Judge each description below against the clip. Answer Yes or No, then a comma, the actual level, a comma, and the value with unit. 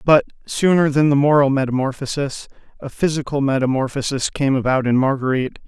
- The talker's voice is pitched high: No, medium, 140 Hz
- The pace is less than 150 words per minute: Yes, average, 140 wpm